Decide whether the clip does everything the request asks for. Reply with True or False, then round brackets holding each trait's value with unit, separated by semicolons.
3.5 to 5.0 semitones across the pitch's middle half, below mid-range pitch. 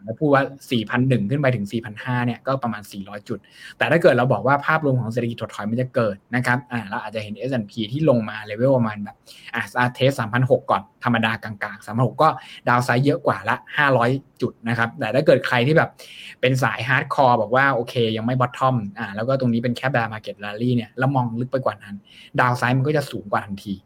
False (2.8 semitones; 120 Hz)